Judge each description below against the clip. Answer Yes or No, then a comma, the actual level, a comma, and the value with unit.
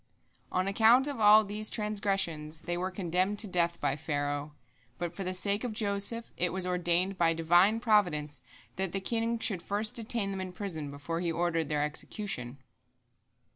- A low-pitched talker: No, medium, 185 Hz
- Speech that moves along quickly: No, average, 175 wpm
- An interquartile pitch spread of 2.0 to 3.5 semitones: No, average, 4.0 semitones